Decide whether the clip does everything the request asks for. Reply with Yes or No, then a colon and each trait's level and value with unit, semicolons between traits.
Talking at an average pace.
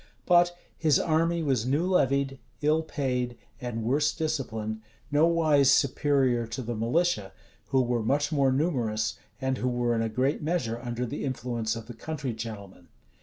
Yes: average, 160 wpm